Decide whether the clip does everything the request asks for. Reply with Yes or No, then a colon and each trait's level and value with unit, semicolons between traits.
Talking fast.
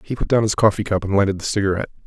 Yes: fast, 290 wpm